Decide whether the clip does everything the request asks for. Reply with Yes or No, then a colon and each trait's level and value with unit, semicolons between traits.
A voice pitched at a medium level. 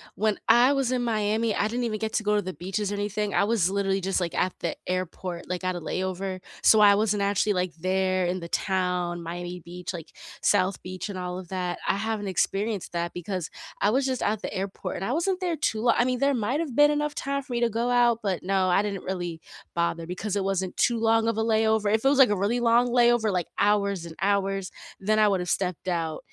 No: high, 200 Hz